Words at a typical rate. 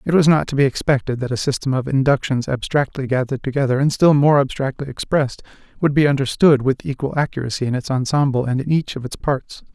No: fast, 210 wpm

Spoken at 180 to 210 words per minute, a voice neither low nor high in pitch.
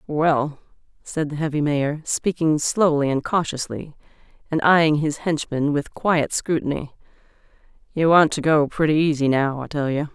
No: average, 155 wpm; medium, 150 Hz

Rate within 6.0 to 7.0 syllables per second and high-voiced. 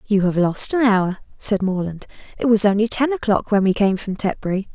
No: 5.3 syllables/s; high, 205 Hz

